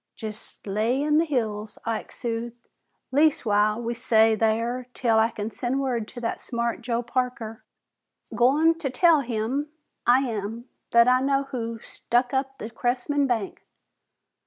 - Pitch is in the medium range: No, high, 240 Hz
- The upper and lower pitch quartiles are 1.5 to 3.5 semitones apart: Yes, average, 2.9 semitones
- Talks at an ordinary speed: Yes, average, 150 wpm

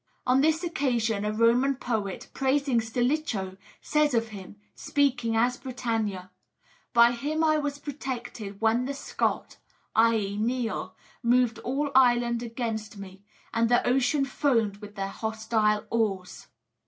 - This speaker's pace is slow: Yes, slow, 130 wpm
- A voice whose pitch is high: Yes, high, 235 Hz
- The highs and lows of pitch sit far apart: No, average, 3.5 semitones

